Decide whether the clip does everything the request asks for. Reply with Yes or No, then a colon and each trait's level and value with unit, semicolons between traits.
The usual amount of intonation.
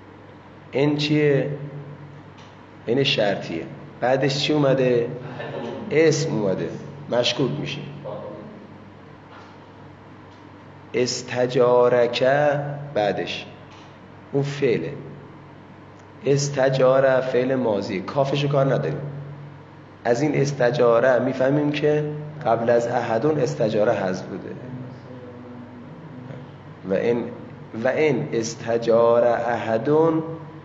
Yes: average, 3.4 semitones